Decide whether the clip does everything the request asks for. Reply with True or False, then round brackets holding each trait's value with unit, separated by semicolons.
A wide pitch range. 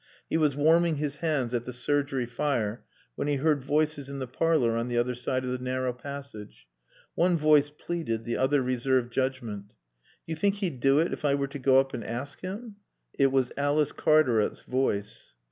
False (3.2 semitones)